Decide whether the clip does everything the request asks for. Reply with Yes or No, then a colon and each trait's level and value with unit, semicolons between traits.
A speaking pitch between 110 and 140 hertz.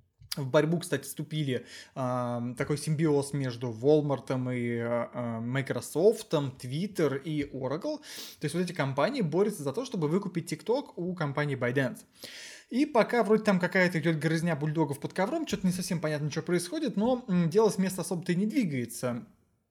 No: medium, 155 Hz